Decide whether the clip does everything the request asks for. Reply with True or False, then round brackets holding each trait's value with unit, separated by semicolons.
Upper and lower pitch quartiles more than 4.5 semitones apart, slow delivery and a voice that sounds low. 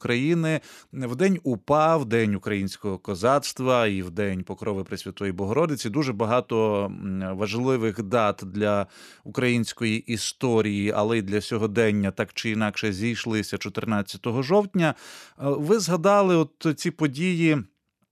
True (5.5 semitones; 120 wpm; 115 Hz)